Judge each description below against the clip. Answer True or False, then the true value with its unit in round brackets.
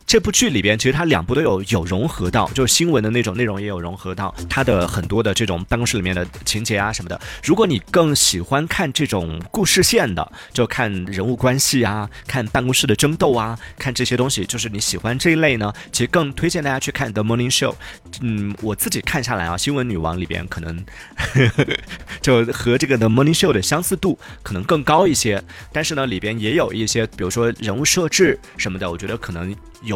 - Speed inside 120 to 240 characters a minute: False (365 characters per minute)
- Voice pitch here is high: False (115 Hz)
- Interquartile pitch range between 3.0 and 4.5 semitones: False (5.3 semitones)